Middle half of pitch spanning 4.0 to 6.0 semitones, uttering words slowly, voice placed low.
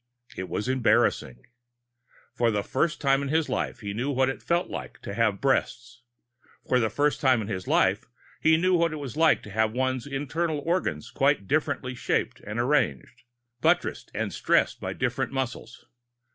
No: average, 5.0 semitones; average, 175 wpm; low, 130 Hz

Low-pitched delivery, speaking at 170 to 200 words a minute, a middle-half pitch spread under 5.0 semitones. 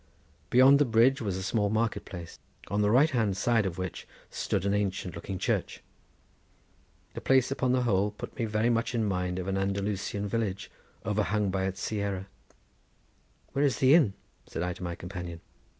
Yes: low, 100 Hz; average, 180 wpm; average, 3.6 semitones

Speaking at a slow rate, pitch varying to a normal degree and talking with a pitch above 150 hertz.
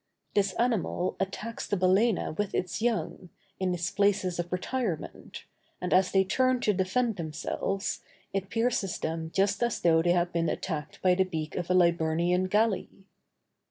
No: average, 160 wpm; average, 3.1 semitones; medium, 185 Hz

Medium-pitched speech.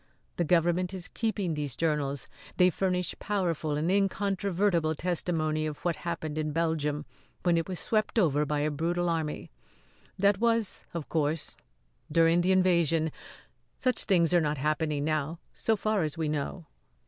Yes: medium, 165 Hz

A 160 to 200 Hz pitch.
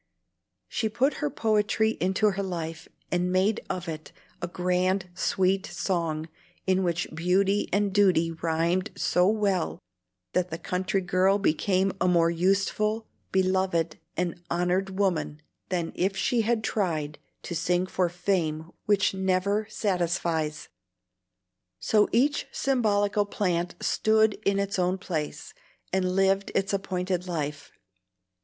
Yes: medium, 185 Hz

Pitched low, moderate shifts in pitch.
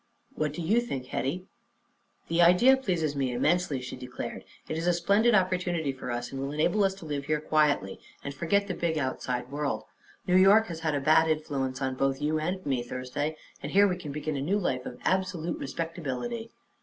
No: medium, 155 Hz; average, 4.8 semitones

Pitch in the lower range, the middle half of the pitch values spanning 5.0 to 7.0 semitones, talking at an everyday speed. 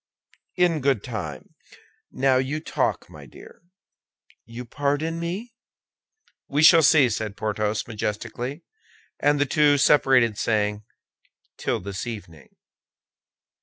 No: low, 130 Hz; wide, 5.6 semitones; slow, 110 wpm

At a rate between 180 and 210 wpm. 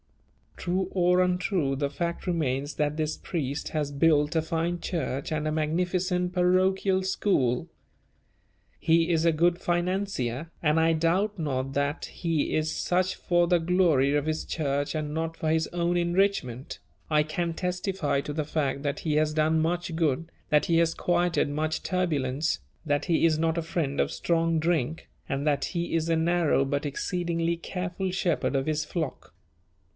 No: average, 170 wpm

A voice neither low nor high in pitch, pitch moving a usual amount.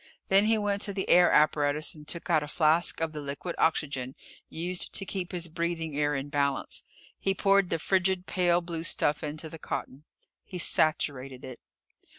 Yes: medium, 165 Hz; average, 3.4 semitones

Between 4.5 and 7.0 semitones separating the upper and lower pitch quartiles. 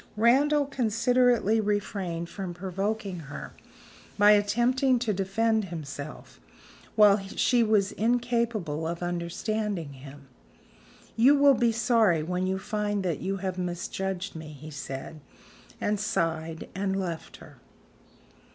Yes: average, 4.8 semitones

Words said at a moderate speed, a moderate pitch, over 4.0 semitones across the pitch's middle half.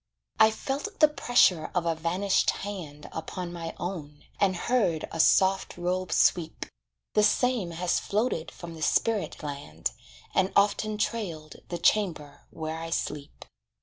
Yes: average, 145 wpm; medium, 175 Hz; average, 4.4 semitones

